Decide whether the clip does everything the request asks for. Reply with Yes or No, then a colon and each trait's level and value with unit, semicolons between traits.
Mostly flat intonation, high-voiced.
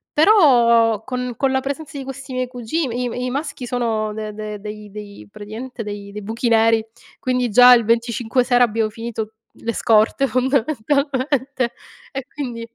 No: average, 3.0 semitones; high, 240 Hz